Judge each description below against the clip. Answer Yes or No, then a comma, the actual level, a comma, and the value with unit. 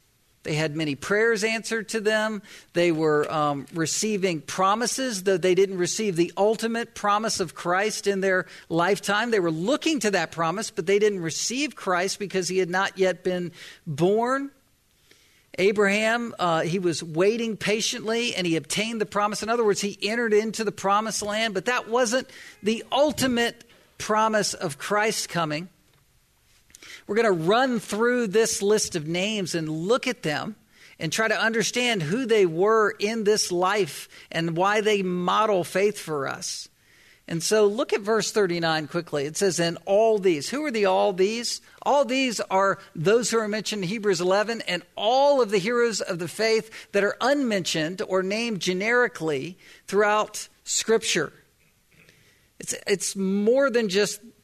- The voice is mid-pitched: No, high, 205 Hz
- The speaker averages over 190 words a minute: No, average, 165 wpm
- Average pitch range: Yes, average, 3.6 semitones